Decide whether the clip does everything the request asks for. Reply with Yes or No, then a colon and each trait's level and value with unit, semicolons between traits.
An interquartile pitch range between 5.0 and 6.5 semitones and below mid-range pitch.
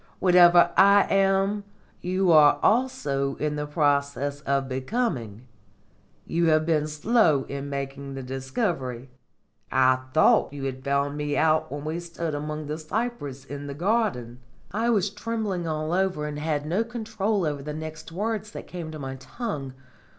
No: wide, 5.6 semitones; medium, 155 Hz